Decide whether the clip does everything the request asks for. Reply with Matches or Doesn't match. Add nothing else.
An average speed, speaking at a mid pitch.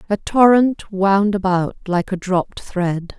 Doesn't match